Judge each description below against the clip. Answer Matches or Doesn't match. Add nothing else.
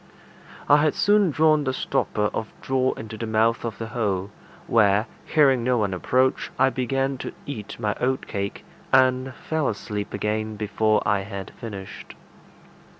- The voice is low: Matches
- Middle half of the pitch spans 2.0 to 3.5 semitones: Doesn't match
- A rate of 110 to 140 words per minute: Doesn't match